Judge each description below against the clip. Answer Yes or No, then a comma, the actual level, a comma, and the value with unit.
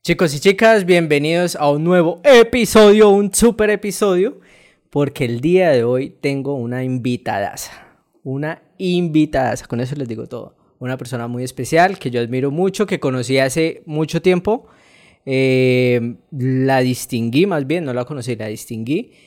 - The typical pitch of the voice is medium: Yes, medium, 145 Hz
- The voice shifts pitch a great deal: Yes, wide, 6.1 semitones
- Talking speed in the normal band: Yes, average, 155 wpm